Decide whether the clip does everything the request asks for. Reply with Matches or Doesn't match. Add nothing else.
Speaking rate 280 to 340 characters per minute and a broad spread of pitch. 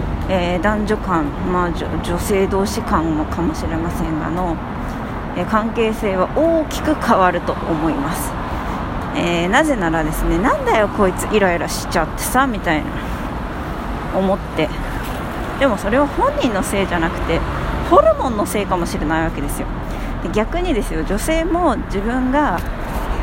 Matches